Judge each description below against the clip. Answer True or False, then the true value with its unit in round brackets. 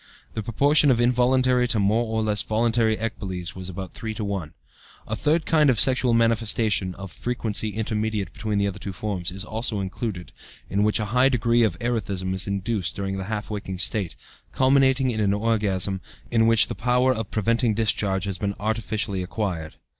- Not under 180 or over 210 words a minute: True (185 wpm)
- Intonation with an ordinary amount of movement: True (3.1 semitones)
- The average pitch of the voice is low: True (110 Hz)